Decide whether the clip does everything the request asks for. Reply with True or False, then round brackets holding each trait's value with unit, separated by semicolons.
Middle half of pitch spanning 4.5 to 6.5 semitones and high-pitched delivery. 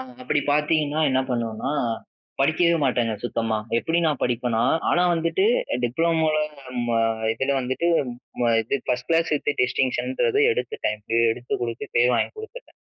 False (5.4 semitones; 135 Hz)